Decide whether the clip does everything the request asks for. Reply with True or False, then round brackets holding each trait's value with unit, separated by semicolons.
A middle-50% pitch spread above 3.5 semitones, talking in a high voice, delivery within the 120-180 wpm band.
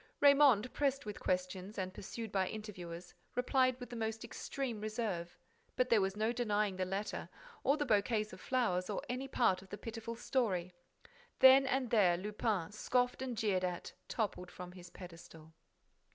True (5.0 semitones; 215 Hz; 165 wpm)